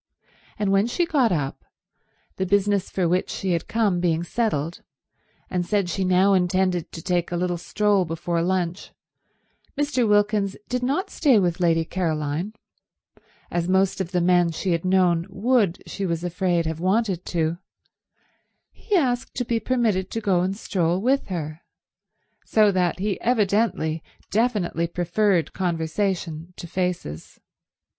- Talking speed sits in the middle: Yes, average, 145 wpm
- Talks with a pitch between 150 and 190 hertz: Yes, medium, 185 Hz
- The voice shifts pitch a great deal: No, average, 3.4 semitones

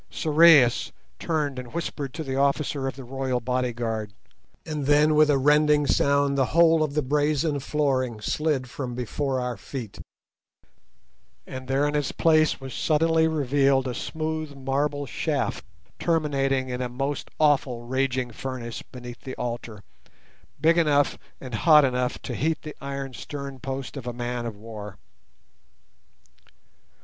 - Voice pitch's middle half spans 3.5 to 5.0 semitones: No, average, 3.0 semitones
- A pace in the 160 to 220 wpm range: No, average, 145 wpm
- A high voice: No, low, 135 Hz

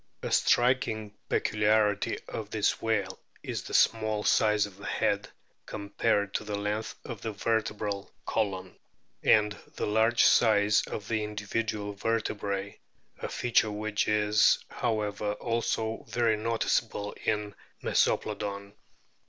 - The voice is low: Yes, low, 105 Hz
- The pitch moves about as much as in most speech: No, narrow, 1.3 semitones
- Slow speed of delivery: Yes, slow, 125 wpm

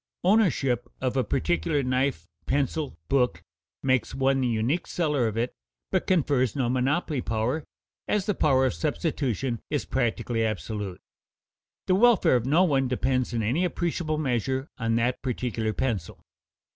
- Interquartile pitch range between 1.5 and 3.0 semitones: No, average, 4.3 semitones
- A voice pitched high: No, low, 130 Hz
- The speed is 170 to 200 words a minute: No, average, 145 wpm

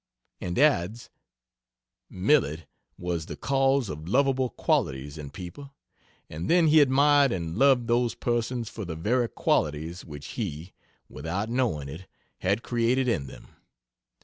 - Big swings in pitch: Yes, wide, 8.2 semitones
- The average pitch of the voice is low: Yes, low, 110 Hz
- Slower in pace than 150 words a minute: Yes, slow, 135 wpm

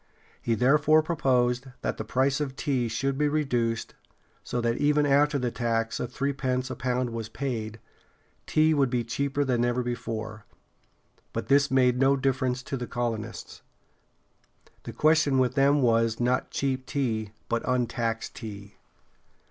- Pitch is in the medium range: No, low, 125 Hz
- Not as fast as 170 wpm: Yes, average, 150 wpm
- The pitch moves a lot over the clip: No, average, 3.0 semitones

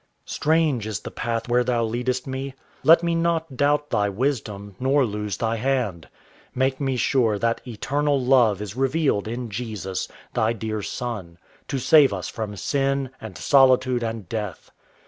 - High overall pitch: No, low, 125 Hz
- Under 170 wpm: Yes, average, 160 wpm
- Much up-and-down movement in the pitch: No, average, 4.0 semitones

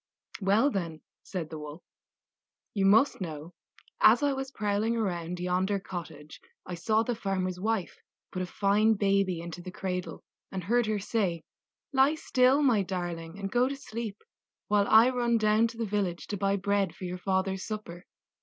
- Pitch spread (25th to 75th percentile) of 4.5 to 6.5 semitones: No, average, 3.7 semitones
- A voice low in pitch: No, high, 195 Hz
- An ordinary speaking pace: Yes, average, 175 wpm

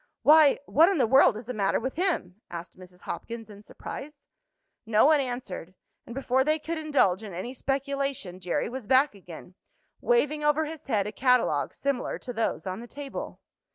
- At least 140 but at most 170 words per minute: No, average, 185 wpm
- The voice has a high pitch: Yes, very high, 255 Hz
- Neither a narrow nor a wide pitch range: No, wide, 5.8 semitones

